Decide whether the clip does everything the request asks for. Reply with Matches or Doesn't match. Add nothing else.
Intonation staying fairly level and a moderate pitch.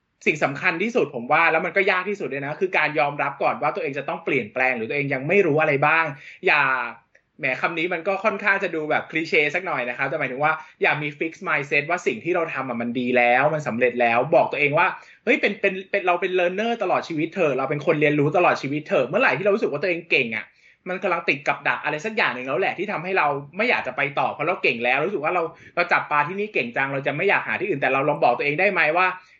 Doesn't match